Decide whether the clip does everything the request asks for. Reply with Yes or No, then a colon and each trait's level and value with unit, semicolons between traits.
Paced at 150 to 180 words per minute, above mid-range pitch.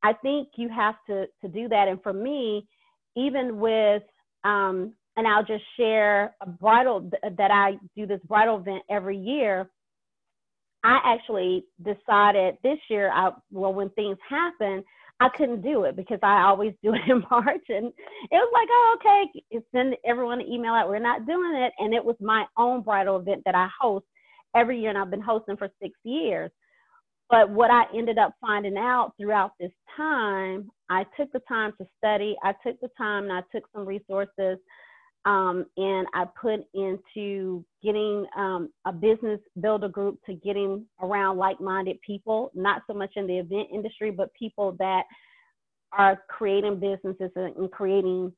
Yes: average, 175 wpm; high, 210 Hz